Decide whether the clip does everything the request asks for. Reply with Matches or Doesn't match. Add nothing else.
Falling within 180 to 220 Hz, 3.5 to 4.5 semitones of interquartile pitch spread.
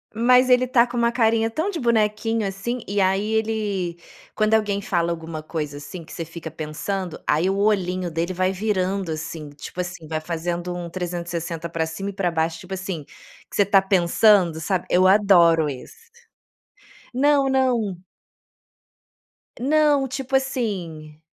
Doesn't match